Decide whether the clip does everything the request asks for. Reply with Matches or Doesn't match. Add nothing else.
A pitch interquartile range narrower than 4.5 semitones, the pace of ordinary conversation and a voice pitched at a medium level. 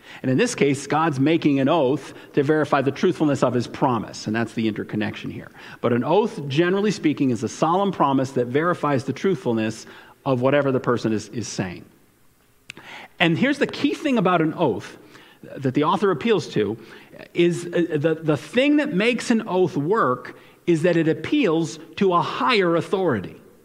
Doesn't match